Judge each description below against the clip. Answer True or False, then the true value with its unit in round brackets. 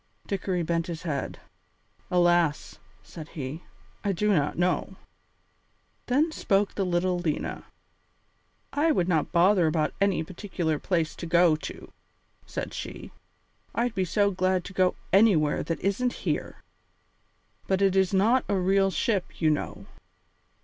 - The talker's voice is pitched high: False (180 Hz)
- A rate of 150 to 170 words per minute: False (140 wpm)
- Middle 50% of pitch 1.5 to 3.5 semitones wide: True (2.9 semitones)